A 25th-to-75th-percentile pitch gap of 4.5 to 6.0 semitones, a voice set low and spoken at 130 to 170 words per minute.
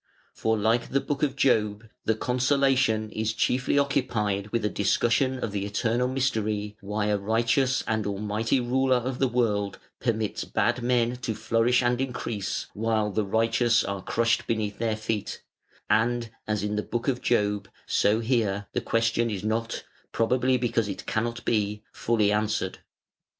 No: average, 2.7 semitones; low, 115 Hz; average, 160 wpm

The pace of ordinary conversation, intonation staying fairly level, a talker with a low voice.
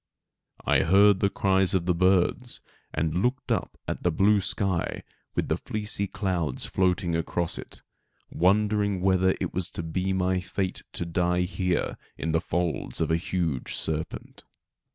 Yes: average, 155 wpm; narrow, 2.2 semitones; very low, 90 Hz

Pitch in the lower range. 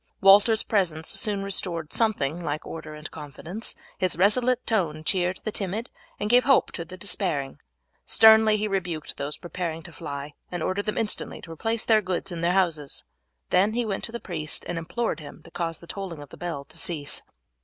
No: medium, 180 Hz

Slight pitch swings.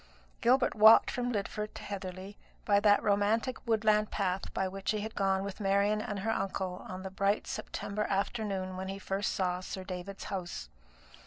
Yes: narrow, 1.9 semitones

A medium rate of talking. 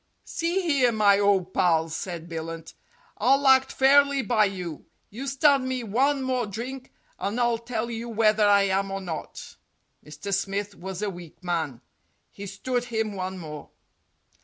Yes: average, 160 wpm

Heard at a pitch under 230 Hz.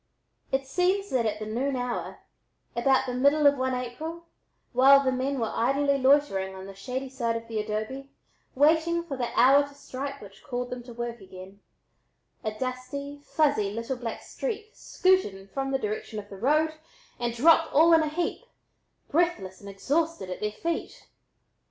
No: very high, 260 Hz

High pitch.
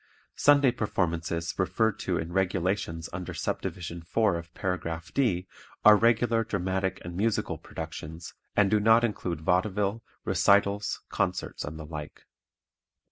No: very low, 95 Hz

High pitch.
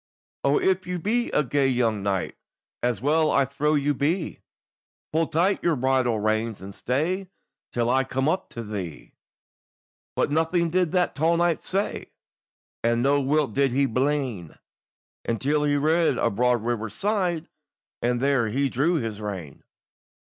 No: medium, 140 Hz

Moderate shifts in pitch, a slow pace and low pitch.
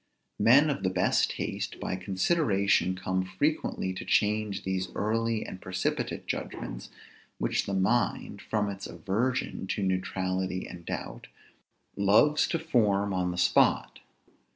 Yes: average, 3.4 semitones; slow, 130 wpm; low, 100 Hz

